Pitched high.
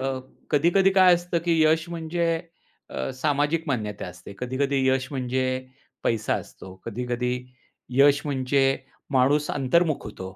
No: medium, 140 Hz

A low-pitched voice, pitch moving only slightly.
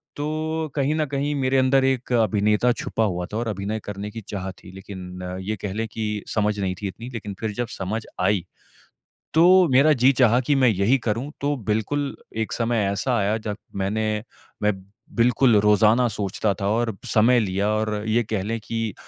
No: low, 110 Hz; average, 3.6 semitones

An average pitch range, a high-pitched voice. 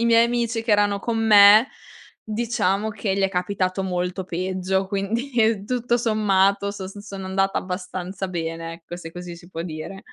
Yes: average, 3.1 semitones; high, 195 Hz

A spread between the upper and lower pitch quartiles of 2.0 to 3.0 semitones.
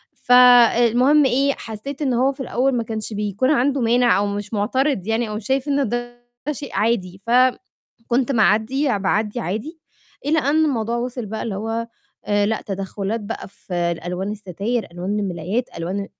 No: average, 3.8 semitones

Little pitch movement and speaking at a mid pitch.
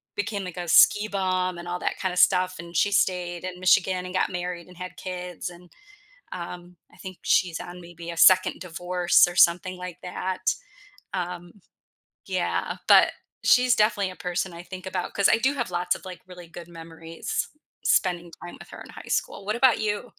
Yes: narrow, 1.3 semitones; medium, 180 Hz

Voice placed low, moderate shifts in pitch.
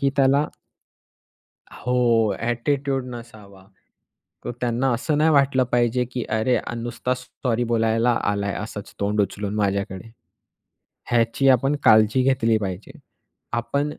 Yes: low, 120 Hz; average, 3.4 semitones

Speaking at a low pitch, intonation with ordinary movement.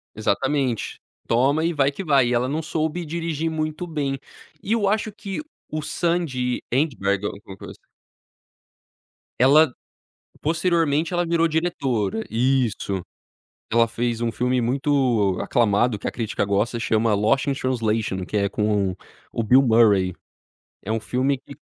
No: low, 130 Hz; wide, 5.8 semitones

